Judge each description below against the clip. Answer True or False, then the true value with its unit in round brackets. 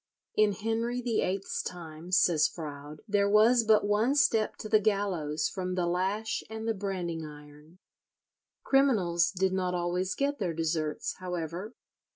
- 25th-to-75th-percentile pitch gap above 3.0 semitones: True (4.1 semitones)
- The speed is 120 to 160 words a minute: True (145 wpm)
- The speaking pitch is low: False (190 Hz)